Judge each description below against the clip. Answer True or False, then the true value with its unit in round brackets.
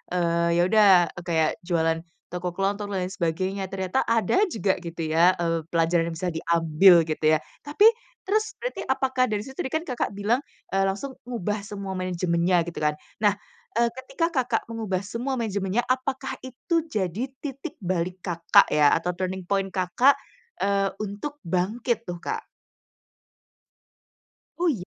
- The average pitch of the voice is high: True (195 Hz)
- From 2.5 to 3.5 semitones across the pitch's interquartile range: False (5.5 semitones)